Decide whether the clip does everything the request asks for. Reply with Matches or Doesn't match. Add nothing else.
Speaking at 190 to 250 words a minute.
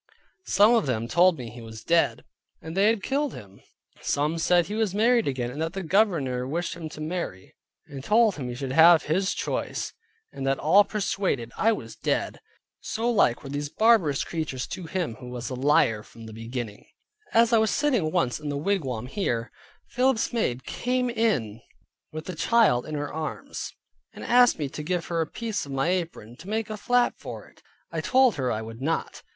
Matches